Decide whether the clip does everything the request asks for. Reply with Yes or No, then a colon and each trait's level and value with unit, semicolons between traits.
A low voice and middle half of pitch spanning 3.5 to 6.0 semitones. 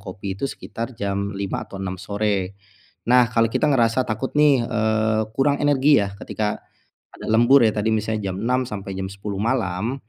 Yes: low, 110 Hz; average, 3.9 semitones